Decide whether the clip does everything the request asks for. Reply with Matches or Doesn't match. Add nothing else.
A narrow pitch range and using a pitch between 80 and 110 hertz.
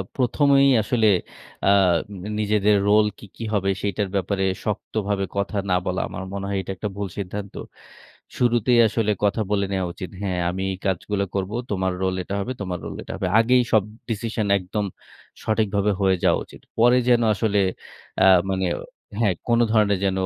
Matches